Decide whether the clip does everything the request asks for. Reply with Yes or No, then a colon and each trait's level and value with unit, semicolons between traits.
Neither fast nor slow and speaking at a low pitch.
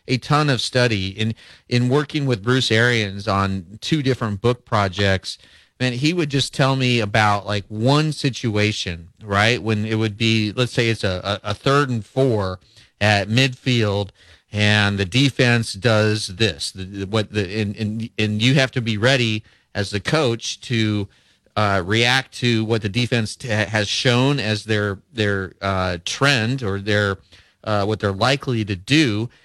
Yes: average, 170 wpm; low, 110 Hz